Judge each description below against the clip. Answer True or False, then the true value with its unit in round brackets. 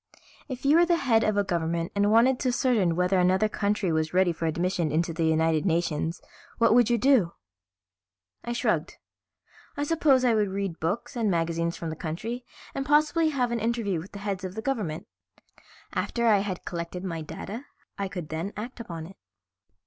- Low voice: False (195 Hz)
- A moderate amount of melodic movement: False (5.9 semitones)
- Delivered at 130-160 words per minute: False (190 wpm)